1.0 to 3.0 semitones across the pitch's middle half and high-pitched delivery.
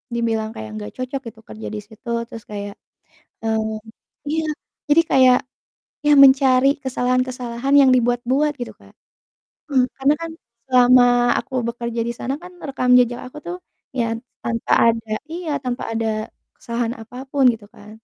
Yes: narrow, 2.5 semitones; high, 245 Hz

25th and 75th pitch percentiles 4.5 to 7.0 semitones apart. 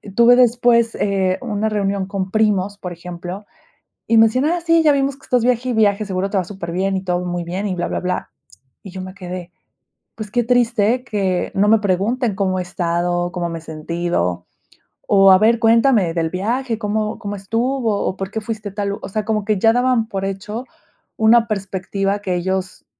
No: average, 3.5 semitones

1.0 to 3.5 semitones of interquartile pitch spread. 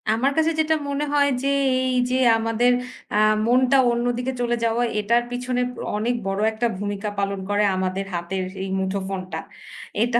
No: average, 3.9 semitones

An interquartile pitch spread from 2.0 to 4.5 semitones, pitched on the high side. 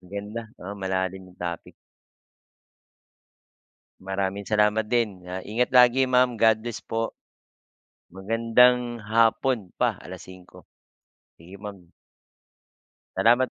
No: average, 3.7 semitones; low, 105 Hz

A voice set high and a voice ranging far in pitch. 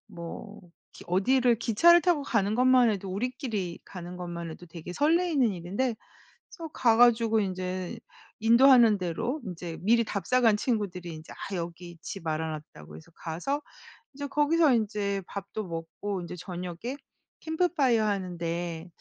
Yes: high, 200 Hz; wide, 6.1 semitones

